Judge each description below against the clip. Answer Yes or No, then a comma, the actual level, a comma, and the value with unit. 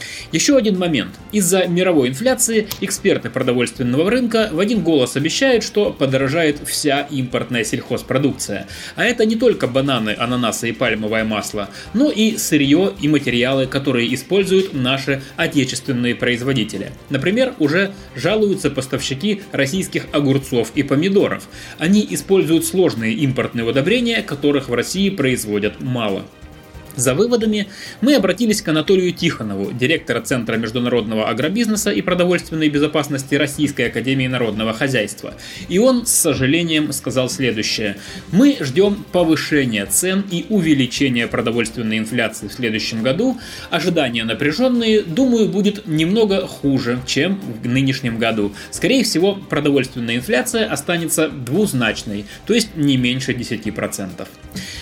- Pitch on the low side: No, medium, 145 Hz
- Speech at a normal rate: Yes, average, 120 wpm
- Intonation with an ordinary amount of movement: No, wide, 7.8 semitones